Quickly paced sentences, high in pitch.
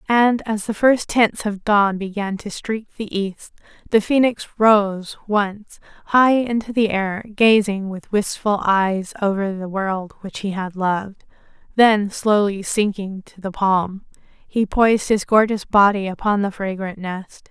No: average, 160 wpm; high, 205 Hz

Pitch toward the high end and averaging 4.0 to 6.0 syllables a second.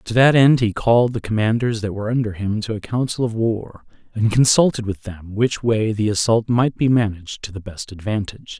No: low, 110 Hz; 5.5 syllables/s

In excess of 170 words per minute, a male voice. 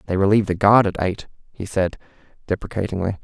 No: average, 165 wpm; male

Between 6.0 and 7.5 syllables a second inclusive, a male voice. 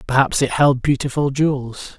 No: 4.9 syllables/s; male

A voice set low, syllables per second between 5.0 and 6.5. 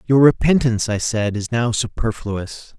No: low, 115 Hz; 4.6 syllables/s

